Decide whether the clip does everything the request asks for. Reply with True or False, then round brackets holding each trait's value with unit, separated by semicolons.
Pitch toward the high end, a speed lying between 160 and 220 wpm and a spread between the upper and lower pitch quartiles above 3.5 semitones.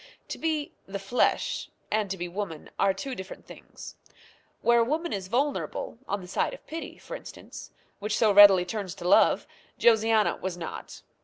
True (205 Hz; 175 wpm; 3.9 semitones)